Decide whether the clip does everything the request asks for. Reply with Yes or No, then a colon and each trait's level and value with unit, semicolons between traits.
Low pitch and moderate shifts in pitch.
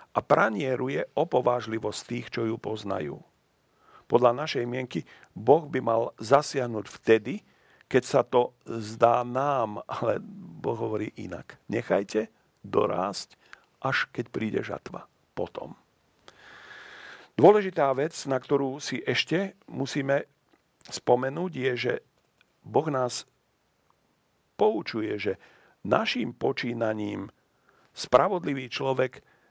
Yes: low, 125 Hz; average, 3.4 semitones